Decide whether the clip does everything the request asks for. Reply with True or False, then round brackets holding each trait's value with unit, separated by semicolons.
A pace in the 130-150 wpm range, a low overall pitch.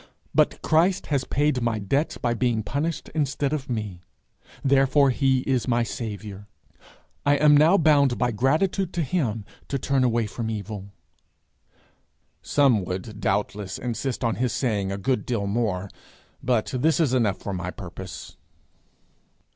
True (145 wpm; 125 Hz)